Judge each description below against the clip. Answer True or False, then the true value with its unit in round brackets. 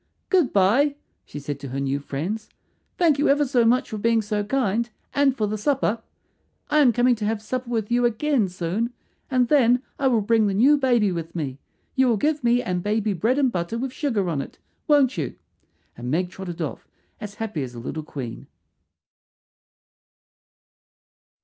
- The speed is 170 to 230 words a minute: True (185 wpm)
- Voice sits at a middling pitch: False (225 Hz)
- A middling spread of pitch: False (6.0 semitones)